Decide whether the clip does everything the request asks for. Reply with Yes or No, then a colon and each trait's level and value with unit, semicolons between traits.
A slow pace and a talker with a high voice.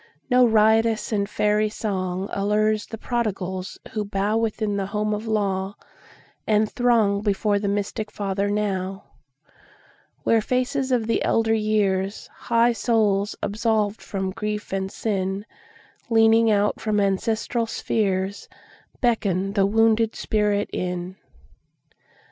Yes: slow, 100 wpm; high, 210 Hz